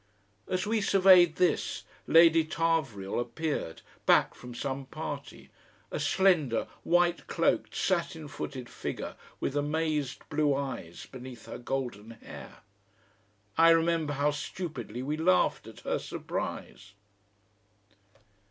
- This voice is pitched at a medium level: Yes, medium, 150 Hz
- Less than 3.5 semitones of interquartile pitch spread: No, average, 4.3 semitones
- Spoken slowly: Yes, slow, 115 wpm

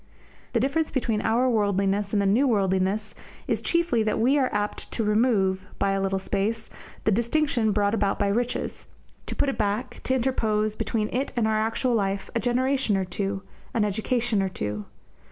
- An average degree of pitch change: Yes, average, 3.4 semitones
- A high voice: Yes, high, 215 Hz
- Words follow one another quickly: No, average, 190 wpm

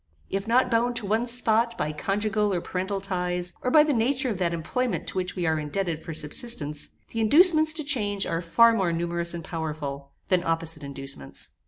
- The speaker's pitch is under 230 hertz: Yes, high, 190 Hz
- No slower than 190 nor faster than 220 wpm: Yes, average, 195 wpm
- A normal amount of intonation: No, wide, 5.9 semitones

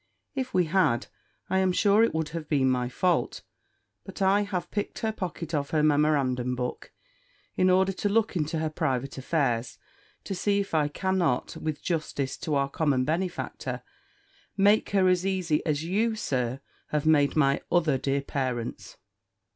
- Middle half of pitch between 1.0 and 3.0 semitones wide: No, wide, 5.4 semitones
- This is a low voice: No, medium, 160 Hz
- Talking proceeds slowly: No, average, 165 wpm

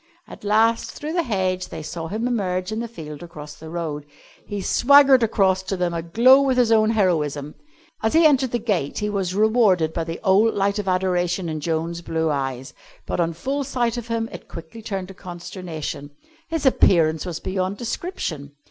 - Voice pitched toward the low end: No, high, 190 Hz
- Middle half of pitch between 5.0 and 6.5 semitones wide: Yes, wide, 5.5 semitones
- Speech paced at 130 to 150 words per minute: No, average, 190 wpm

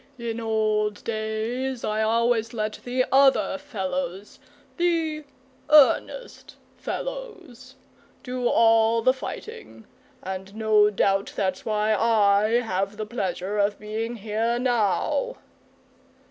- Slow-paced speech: Yes, slow, 105 wpm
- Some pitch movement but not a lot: Yes, average, 3.2 semitones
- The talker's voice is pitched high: Yes, high, 225 Hz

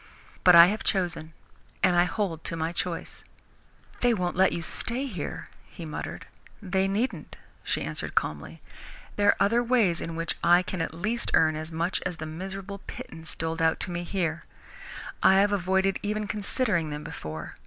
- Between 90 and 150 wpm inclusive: No, average, 175 wpm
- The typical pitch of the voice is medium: Yes, medium, 180 Hz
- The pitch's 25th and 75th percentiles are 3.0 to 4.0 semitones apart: Yes, average, 3.6 semitones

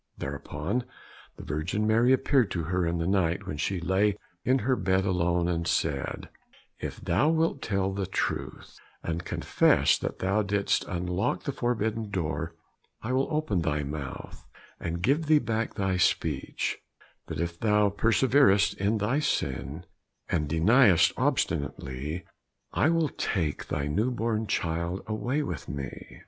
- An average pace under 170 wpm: Yes, average, 150 wpm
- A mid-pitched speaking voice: No, very low, 95 Hz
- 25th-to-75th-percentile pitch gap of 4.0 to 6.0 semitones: Yes, average, 5.2 semitones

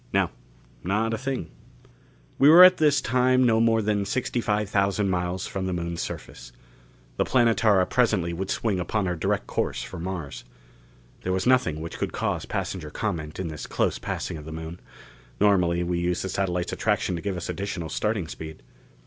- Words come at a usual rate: Yes, average, 185 wpm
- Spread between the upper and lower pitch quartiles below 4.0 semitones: No, average, 4.6 semitones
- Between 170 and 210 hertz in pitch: No, very low, 95 Hz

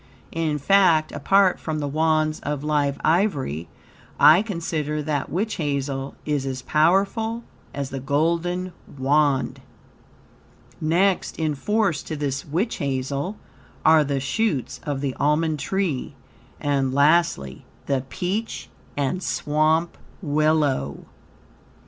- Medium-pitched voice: Yes, medium, 155 Hz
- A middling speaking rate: No, slow, 115 wpm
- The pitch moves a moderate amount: Yes, average, 3.5 semitones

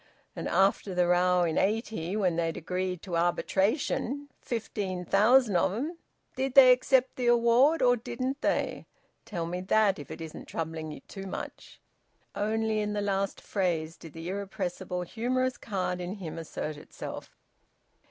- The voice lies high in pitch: Yes, high, 195 Hz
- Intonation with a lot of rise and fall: No, average, 4.9 semitones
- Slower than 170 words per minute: Yes, average, 155 wpm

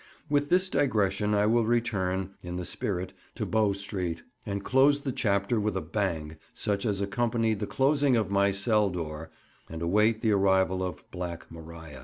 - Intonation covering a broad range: No, average, 3.7 semitones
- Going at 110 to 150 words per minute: No, average, 175 wpm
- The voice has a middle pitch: No, low, 100 Hz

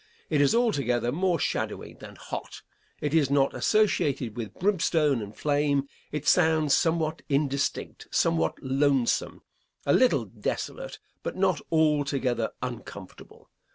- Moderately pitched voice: Yes, medium, 145 Hz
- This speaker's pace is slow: Yes, slow, 120 wpm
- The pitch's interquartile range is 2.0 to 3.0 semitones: No, average, 3.5 semitones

